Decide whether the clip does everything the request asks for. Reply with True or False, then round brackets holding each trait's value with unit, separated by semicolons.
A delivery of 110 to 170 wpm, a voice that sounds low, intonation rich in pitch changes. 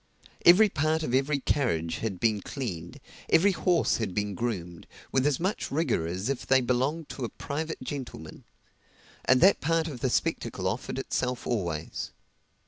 True (160 wpm; 130 Hz; 7.2 semitones)